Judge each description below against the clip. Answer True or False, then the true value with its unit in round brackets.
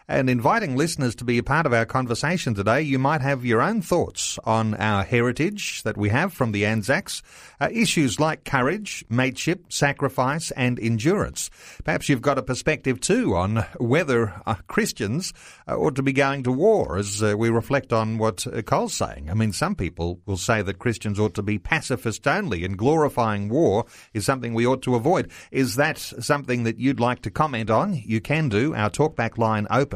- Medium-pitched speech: False (125 Hz)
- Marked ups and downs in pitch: False (4.4 semitones)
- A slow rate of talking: False (195 wpm)